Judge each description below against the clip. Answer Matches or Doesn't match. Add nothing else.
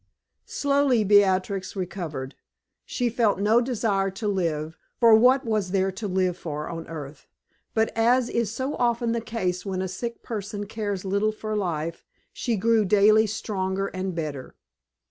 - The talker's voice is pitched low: Doesn't match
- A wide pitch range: Doesn't match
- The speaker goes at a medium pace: Matches